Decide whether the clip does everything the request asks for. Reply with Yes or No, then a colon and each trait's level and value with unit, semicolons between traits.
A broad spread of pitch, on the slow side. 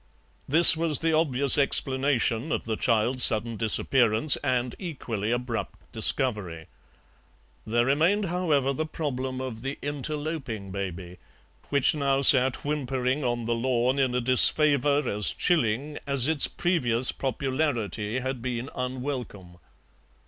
No: average, 3.7 semitones; slow, 125 wpm